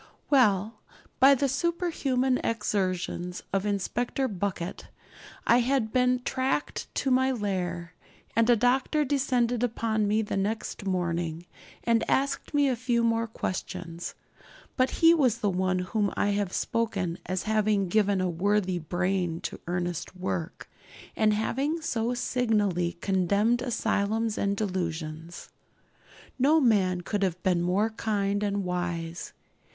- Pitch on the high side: Yes, high, 210 Hz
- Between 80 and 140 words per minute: Yes, slow, 135 wpm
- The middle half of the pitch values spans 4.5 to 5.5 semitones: Yes, average, 5.0 semitones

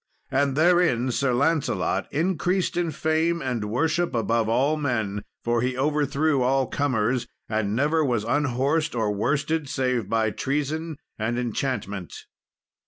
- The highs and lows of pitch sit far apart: No, average, 4.8 semitones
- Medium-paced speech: No, slow, 130 wpm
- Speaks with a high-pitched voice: No, low, 135 Hz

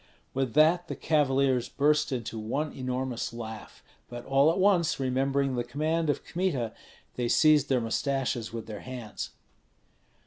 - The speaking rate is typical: Yes, average, 145 wpm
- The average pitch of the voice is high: No, low, 135 Hz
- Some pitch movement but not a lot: Yes, average, 3.9 semitones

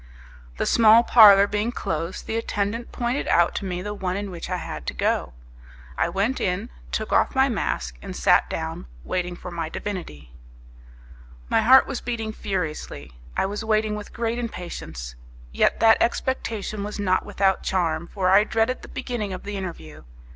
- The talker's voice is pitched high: Yes, high, 200 Hz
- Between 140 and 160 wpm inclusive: No, average, 175 wpm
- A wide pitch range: No, average, 3.9 semitones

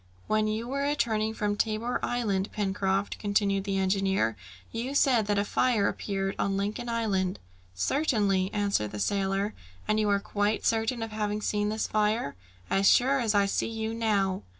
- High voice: Yes, high, 210 Hz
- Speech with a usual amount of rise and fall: No, narrow, 2.3 semitones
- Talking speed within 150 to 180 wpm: Yes, average, 170 wpm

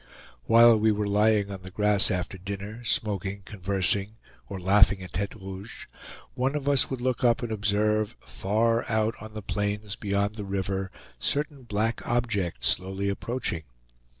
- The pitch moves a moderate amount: No, narrow, 2.3 semitones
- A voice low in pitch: Yes, low, 105 Hz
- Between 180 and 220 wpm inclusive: No, average, 155 wpm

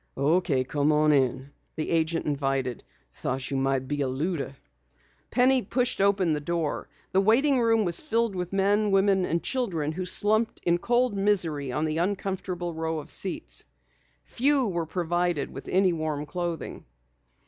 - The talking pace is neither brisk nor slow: Yes, average, 160 wpm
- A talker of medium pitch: Yes, medium, 170 Hz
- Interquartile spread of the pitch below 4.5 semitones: No, average, 5.2 semitones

